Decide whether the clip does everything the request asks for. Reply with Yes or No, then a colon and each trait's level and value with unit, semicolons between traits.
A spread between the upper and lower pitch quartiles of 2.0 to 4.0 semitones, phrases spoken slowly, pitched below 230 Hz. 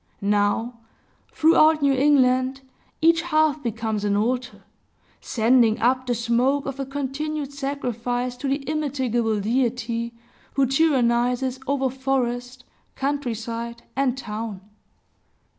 No: average, 2.9 semitones; slow, 110 wpm; very high, 255 Hz